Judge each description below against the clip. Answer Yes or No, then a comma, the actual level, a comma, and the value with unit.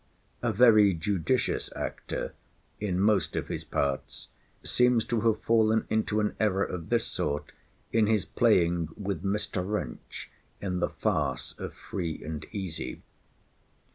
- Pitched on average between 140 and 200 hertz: No, low, 100 Hz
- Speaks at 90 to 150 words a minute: Yes, average, 140 wpm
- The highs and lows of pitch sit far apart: No, average, 3.7 semitones